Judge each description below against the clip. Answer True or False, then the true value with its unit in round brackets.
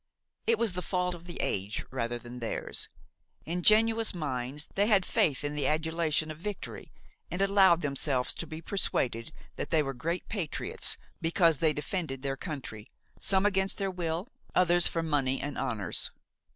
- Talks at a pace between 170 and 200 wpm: False (160 wpm)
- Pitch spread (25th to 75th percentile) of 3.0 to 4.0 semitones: False (5.2 semitones)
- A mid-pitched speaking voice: True (160 Hz)